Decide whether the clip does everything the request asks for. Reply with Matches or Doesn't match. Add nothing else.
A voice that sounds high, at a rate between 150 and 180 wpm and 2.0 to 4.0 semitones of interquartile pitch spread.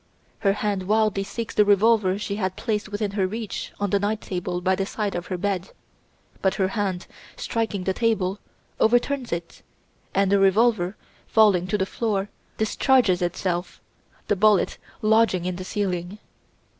Matches